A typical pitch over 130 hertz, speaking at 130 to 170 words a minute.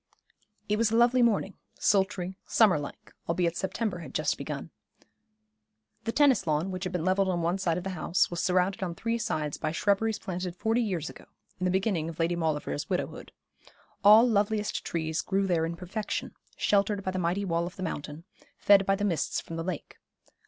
No: medium, 185 Hz; average, 195 wpm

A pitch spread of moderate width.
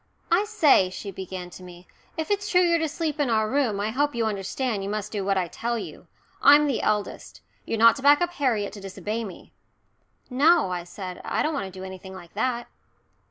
No: wide, 7.0 semitones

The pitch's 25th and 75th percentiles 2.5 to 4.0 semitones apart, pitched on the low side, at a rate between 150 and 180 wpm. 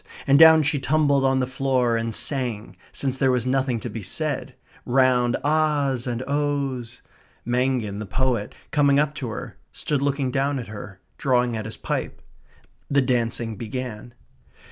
Yes: average, 2.9 semitones; low, 130 Hz; average, 160 wpm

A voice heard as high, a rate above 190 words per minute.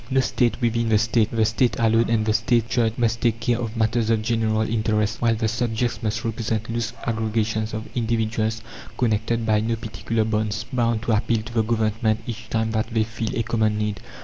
No: low, 110 Hz; average, 200 wpm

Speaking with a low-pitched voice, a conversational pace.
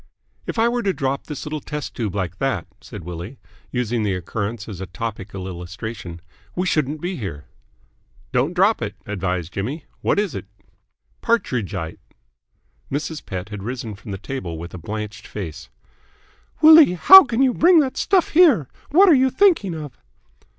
Yes: low, 125 Hz; average, 160 wpm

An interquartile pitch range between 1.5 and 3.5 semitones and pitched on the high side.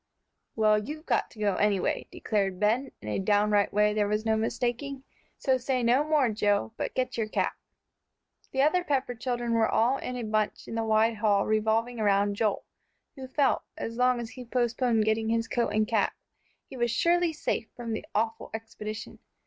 Yes: average, 2.9 semitones; high, 225 Hz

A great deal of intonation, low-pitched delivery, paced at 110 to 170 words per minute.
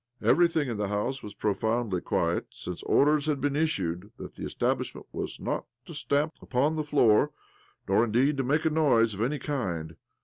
No: wide, 6.1 semitones; low, 130 Hz; average, 180 wpm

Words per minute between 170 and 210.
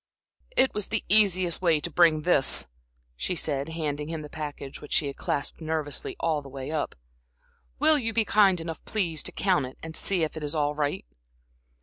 Yes: average, 200 wpm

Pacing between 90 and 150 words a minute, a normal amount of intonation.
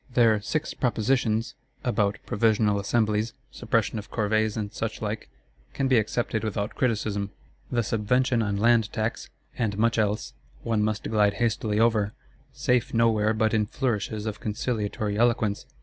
No: average, 140 wpm; narrow, 1.8 semitones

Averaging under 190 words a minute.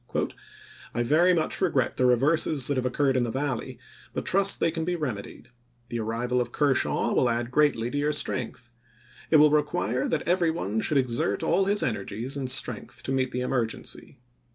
No: average, 195 wpm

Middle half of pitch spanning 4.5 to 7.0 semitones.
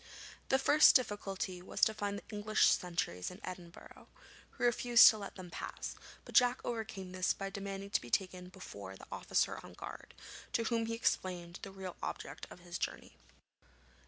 No: average, 3.3 semitones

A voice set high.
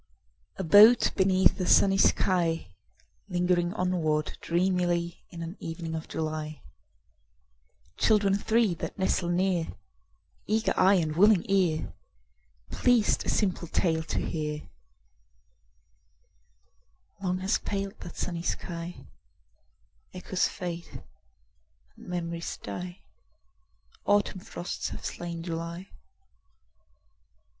No: medium, 175 Hz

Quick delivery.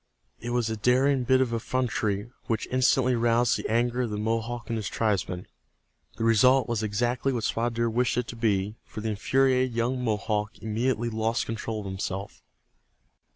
No: average, 175 wpm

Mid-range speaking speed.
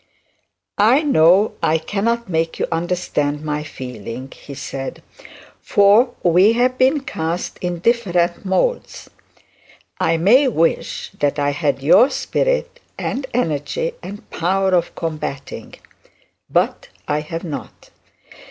No: slow, 120 wpm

